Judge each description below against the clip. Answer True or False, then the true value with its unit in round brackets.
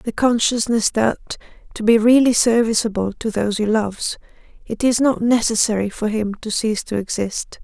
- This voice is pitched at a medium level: False (220 Hz)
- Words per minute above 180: False (165 wpm)